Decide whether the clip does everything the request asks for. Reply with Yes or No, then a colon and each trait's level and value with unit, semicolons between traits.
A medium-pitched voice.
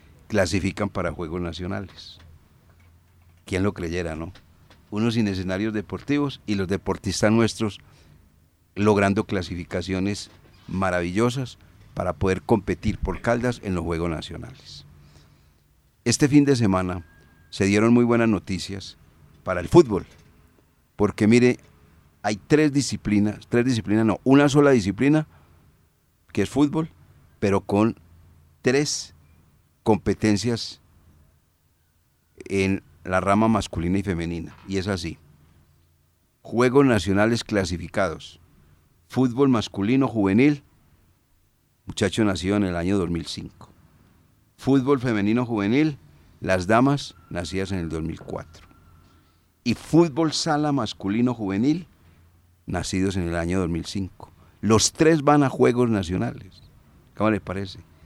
No: very low, 95 Hz